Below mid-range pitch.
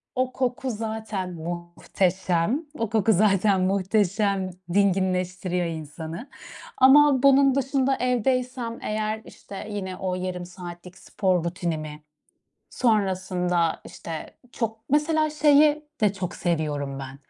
No: high, 195 Hz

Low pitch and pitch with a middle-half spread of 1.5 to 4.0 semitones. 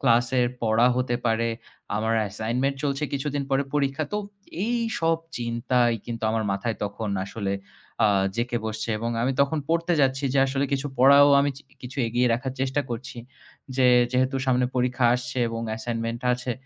Yes: low, 125 Hz; average, 2.8 semitones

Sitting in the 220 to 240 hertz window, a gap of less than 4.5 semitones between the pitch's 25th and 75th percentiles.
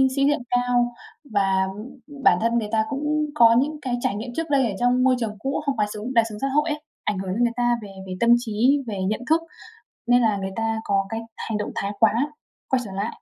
Yes: high, 235 Hz; average, 4.0 semitones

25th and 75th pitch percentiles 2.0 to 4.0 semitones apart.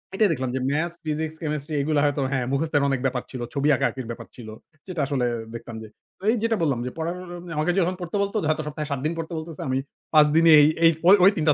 Yes: average, 3.4 semitones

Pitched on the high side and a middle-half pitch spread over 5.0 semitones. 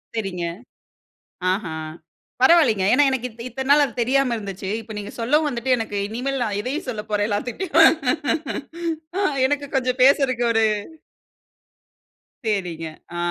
Yes: high, 245 Hz; wide, 5.4 semitones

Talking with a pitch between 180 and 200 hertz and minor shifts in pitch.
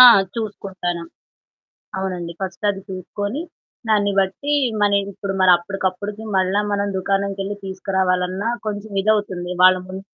Yes: high, 195 Hz; narrow, 1.7 semitones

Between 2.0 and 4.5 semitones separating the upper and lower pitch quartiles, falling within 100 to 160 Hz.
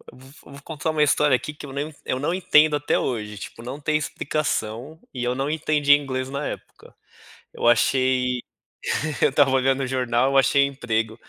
Yes: average, 2.7 semitones; low, 135 Hz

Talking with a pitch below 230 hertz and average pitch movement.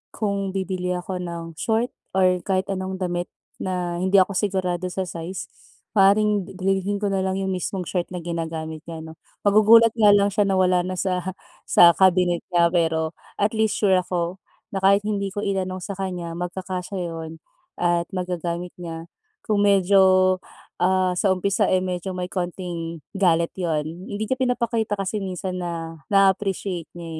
No: medium, 185 Hz; narrow, 2.1 semitones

